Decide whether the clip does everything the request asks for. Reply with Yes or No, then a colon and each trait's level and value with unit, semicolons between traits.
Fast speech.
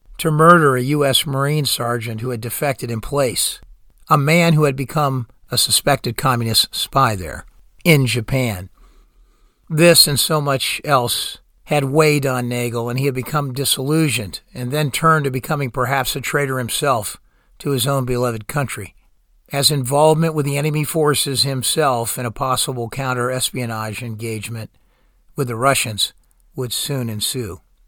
No: average, 150 wpm